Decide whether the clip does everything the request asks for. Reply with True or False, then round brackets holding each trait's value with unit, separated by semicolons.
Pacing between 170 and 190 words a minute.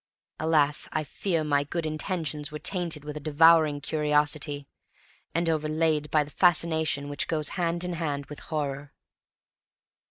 False (140 wpm)